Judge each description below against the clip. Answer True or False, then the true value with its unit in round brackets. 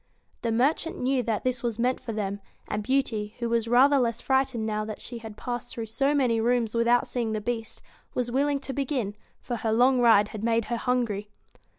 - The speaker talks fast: True (215 wpm)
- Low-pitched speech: False (235 Hz)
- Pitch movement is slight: True (2.3 semitones)